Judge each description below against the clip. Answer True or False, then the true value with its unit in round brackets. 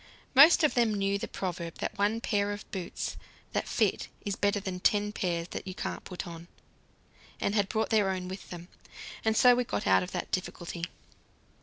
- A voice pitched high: True (200 Hz)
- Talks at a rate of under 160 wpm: False (195 wpm)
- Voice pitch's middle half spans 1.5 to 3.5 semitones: True (3.1 semitones)